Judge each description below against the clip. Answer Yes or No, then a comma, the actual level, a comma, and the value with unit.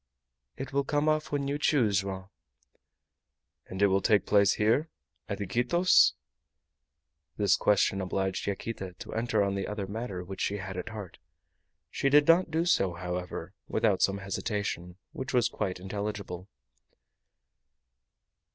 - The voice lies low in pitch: Yes, low, 100 Hz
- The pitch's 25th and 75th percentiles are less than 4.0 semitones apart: No, average, 4.3 semitones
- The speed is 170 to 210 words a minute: No, average, 140 wpm